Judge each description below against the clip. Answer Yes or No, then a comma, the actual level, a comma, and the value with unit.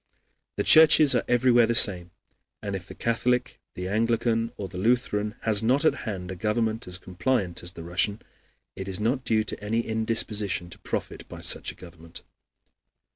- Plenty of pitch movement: No, average, 4.0 semitones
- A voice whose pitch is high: No, low, 110 Hz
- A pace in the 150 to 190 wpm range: Yes, average, 180 wpm